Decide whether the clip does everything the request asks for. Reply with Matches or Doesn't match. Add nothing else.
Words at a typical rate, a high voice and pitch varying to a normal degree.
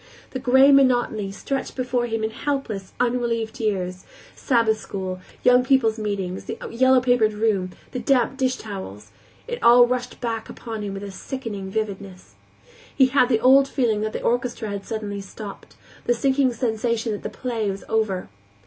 Matches